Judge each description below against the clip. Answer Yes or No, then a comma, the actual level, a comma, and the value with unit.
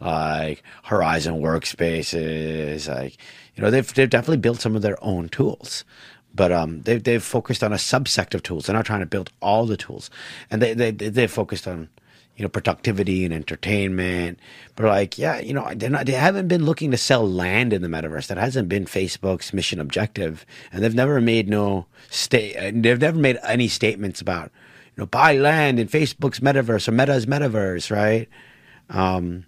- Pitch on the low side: Yes, low, 105 Hz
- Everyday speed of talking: Yes, average, 185 wpm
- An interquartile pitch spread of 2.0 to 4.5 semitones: No, average, 5.1 semitones